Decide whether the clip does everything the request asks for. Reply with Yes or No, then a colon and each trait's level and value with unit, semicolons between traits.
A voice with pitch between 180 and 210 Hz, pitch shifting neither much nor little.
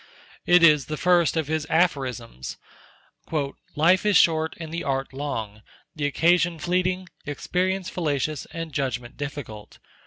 No: medium, 155 Hz; average, 4.0 semitones